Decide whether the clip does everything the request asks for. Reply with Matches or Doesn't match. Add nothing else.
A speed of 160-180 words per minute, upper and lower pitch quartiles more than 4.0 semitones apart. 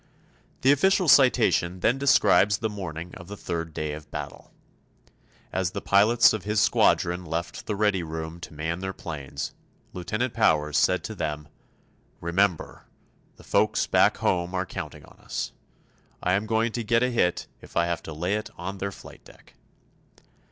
Matches